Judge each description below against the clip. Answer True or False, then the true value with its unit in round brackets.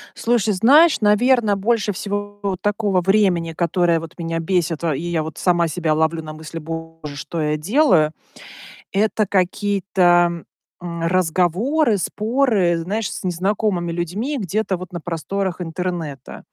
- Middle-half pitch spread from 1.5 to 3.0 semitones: False (3.7 semitones)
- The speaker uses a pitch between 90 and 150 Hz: False (180 Hz)